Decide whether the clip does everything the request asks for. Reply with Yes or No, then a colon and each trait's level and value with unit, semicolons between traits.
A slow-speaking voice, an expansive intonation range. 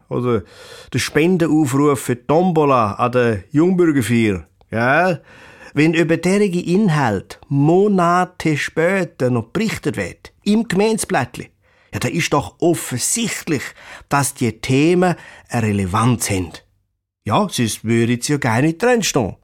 Yes: slow, 120 wpm; wide, 6.9 semitones